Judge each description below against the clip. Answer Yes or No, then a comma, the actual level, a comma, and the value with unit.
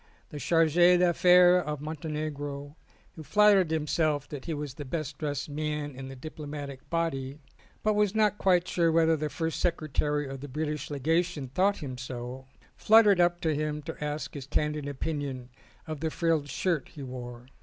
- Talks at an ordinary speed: Yes, average, 175 wpm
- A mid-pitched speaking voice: Yes, medium, 150 Hz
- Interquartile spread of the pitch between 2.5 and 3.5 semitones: Yes, average, 2.9 semitones